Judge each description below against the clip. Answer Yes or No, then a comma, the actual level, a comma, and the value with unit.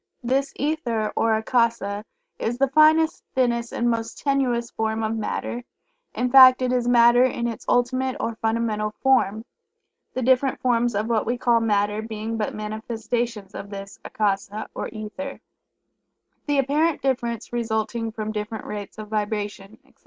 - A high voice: Yes, high, 230 Hz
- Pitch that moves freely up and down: No, average, 2.7 semitones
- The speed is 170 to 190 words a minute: No, average, 155 wpm